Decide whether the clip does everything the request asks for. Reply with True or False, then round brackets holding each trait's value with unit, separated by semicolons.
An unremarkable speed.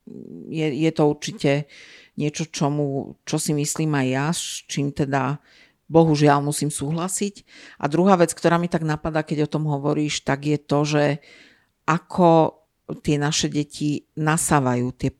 True (150 wpm)